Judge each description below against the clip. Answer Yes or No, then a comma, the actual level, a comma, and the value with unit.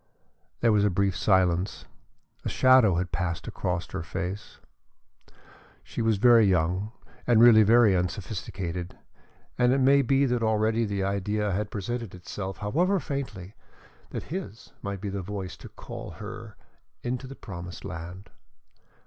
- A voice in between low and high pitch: No, low, 105 Hz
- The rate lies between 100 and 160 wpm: Yes, average, 145 wpm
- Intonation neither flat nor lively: Yes, average, 4.1 semitones